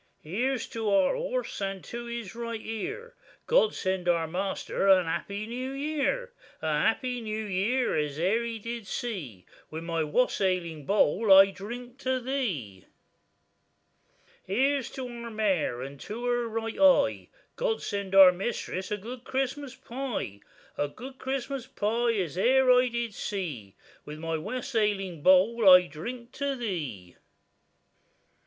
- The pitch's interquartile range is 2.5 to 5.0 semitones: No, wide, 5.4 semitones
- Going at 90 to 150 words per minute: Yes, average, 145 wpm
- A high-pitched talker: Yes, high, 220 Hz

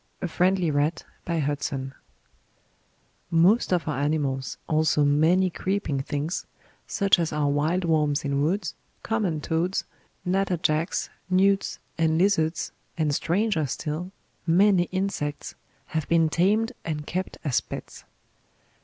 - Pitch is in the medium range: Yes, medium, 165 Hz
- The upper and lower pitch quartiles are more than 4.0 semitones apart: No, average, 3.6 semitones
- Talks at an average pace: No, slow, 120 wpm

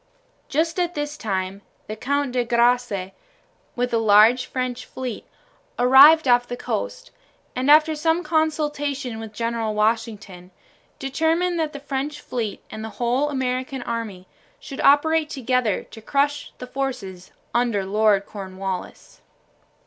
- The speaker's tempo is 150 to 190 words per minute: No, slow, 135 wpm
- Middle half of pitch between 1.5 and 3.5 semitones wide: No, average, 5.0 semitones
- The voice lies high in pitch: Yes, very high, 250 Hz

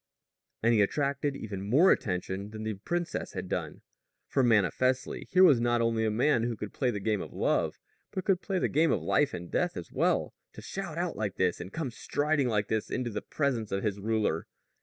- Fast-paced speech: Yes, fast, 215 wpm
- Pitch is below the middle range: Yes, low, 115 Hz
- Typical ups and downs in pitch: No, wide, 5.7 semitones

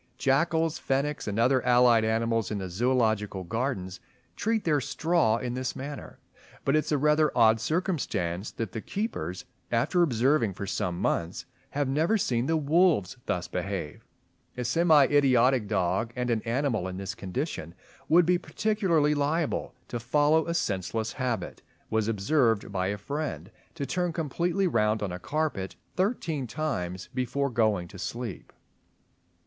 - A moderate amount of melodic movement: No, wide, 6.5 semitones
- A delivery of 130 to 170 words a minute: Yes, average, 150 wpm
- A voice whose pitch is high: No, low, 125 Hz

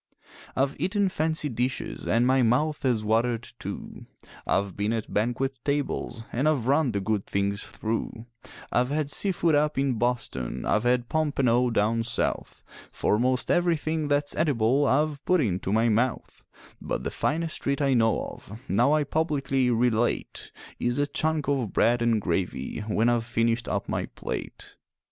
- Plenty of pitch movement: No, average, 4.2 semitones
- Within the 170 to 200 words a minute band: No, average, 160 wpm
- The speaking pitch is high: No, low, 125 Hz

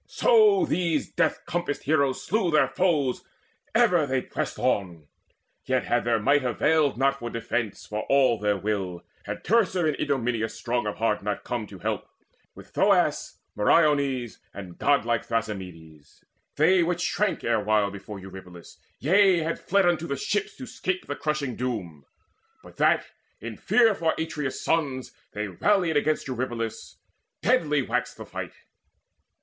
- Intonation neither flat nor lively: No, wide, 7.3 semitones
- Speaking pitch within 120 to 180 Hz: Yes, low, 135 Hz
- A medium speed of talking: Yes, average, 150 wpm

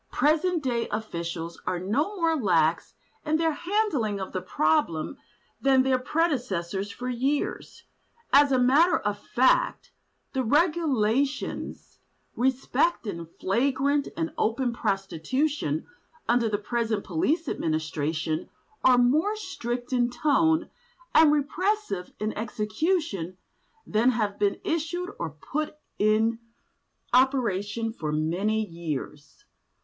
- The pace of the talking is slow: Yes, slow, 115 wpm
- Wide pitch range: Yes, wide, 7.1 semitones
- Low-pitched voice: No, high, 240 Hz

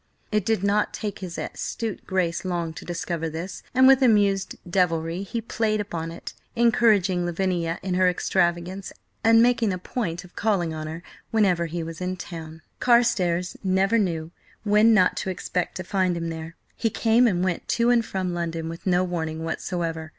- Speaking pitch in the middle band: Yes, medium, 180 Hz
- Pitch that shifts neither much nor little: Yes, average, 3.8 semitones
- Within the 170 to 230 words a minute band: Yes, average, 180 wpm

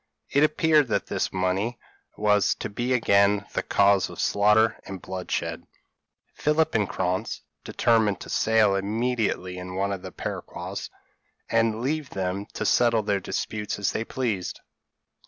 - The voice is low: Yes, low, 105 Hz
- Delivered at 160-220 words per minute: No, average, 145 wpm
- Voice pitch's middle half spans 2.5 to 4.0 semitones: Yes, average, 3.2 semitones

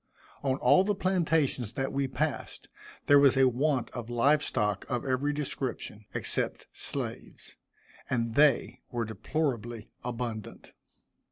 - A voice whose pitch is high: No, low, 130 Hz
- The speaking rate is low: Yes, slow, 125 wpm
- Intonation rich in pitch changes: No, average, 3.7 semitones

